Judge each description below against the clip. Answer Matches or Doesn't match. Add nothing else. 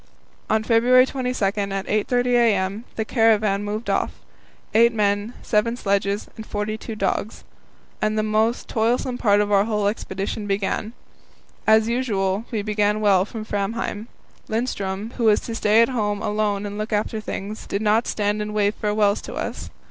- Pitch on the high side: Matches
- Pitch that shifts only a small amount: Matches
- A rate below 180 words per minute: Matches